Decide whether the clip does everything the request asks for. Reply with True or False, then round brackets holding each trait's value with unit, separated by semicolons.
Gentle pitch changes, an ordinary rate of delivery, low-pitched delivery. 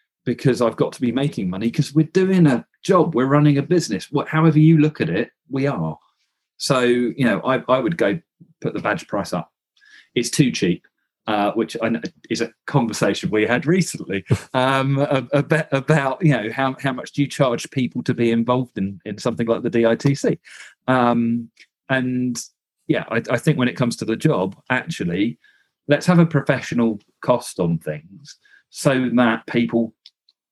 False (3.8 semitones; 185 wpm; 130 Hz)